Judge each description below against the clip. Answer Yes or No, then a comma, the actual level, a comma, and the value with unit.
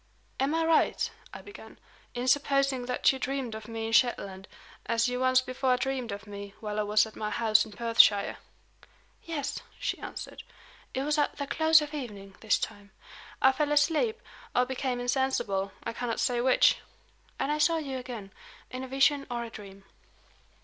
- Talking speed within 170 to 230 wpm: Yes, average, 180 wpm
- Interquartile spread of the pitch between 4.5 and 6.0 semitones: No, average, 4.0 semitones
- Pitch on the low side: No, very high, 250 Hz